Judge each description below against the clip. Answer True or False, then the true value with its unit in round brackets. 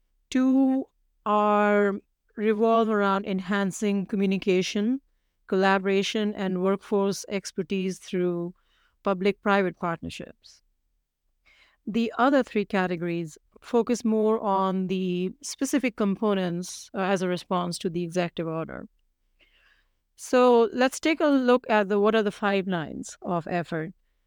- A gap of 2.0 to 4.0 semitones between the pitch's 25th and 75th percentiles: True (3.3 semitones)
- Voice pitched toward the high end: True (200 Hz)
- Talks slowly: True (110 wpm)